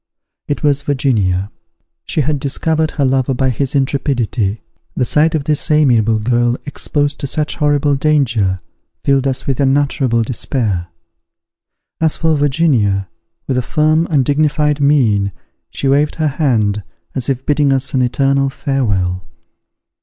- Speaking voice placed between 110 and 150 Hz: Yes, low, 135 Hz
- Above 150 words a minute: No, average, 140 wpm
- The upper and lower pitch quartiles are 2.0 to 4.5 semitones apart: Yes, average, 3.6 semitones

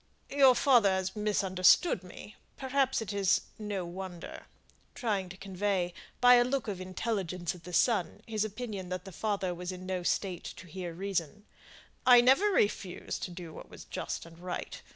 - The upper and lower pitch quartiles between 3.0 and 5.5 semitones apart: Yes, average, 3.5 semitones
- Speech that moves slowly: No, average, 175 wpm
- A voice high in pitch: Yes, high, 195 Hz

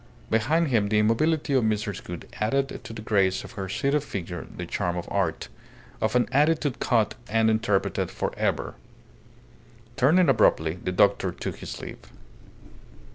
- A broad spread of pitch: Yes, wide, 5.7 semitones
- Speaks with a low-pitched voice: Yes, low, 110 Hz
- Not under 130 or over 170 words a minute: Yes, average, 155 wpm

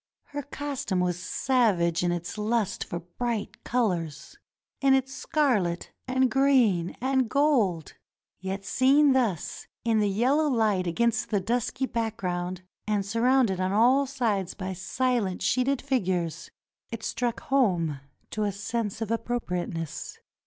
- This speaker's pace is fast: No, slow, 135 wpm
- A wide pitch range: Yes, wide, 5.7 semitones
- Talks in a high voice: Yes, high, 220 Hz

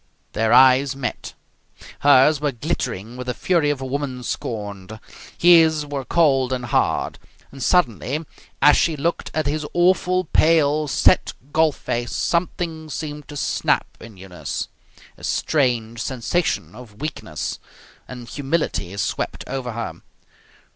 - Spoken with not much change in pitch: No, average, 4.4 semitones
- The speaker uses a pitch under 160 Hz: Yes, medium, 140 Hz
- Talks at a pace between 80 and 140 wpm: Yes, slow, 135 wpm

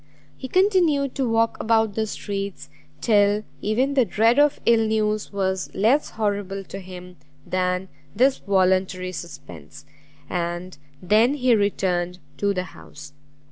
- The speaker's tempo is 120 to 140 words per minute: Yes, slow, 135 wpm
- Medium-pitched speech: No, high, 205 Hz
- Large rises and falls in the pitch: No, average, 3.8 semitones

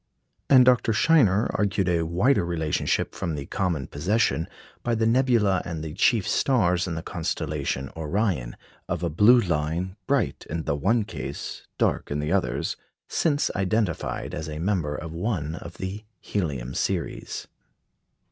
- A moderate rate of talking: Yes, average, 150 wpm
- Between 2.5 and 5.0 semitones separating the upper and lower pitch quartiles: No, wide, 5.4 semitones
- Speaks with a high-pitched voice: No, very low, 90 Hz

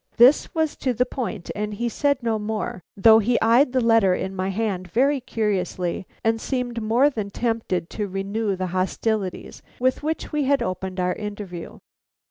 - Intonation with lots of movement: No, average, 4.2 semitones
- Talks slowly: No, average, 175 wpm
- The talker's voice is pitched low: No, high, 220 Hz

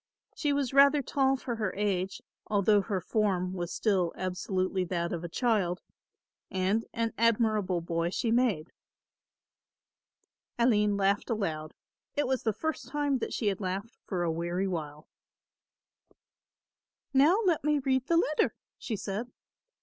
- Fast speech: No, average, 140 wpm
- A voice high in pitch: Yes, high, 210 Hz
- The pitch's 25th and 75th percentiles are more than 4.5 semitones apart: Yes, wide, 5.4 semitones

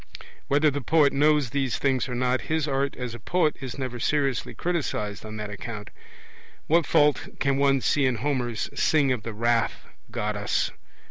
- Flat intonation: No, average, 3.7 semitones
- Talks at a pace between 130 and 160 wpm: No, average, 175 wpm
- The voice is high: No, low, 130 Hz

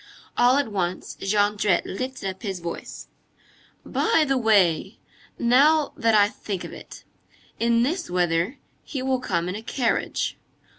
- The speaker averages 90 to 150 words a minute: Yes, average, 145 wpm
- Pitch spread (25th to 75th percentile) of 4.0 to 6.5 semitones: Yes, average, 5.3 semitones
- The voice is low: No, high, 220 Hz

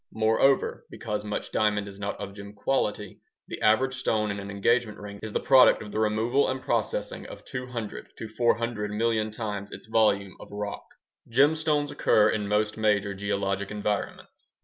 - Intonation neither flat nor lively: No, narrow, 2.3 semitones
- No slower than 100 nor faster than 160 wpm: No, average, 170 wpm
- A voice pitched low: Yes, low, 105 Hz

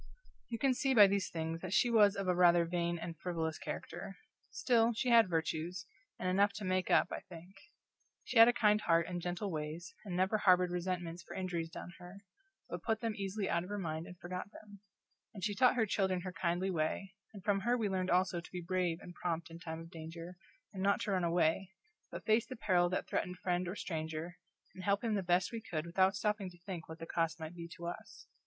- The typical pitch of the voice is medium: Yes, medium, 180 Hz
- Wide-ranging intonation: No, average, 2.9 semitones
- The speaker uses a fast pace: Yes, fast, 230 wpm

